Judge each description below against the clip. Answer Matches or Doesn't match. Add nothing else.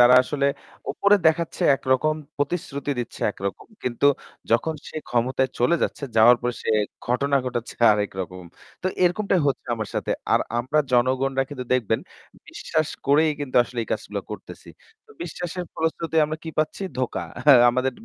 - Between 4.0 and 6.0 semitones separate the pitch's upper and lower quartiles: Matches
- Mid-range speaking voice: Doesn't match